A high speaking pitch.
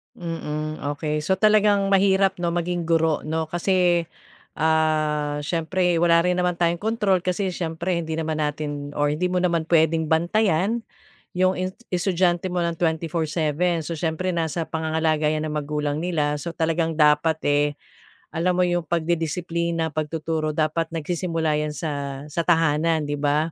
No: medium, 165 Hz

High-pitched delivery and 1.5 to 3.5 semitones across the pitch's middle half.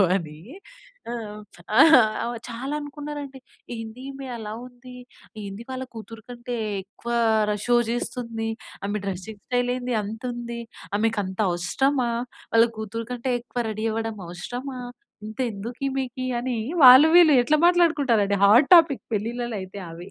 Yes: high, 235 Hz; average, 3.2 semitones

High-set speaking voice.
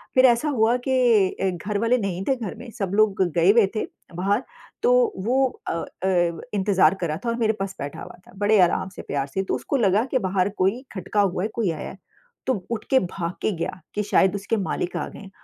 Yes: high, 205 Hz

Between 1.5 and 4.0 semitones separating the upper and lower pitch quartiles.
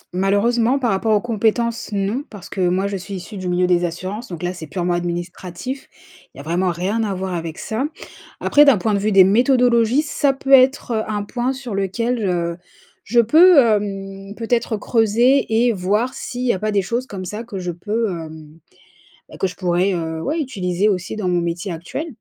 No: average, 4.8 semitones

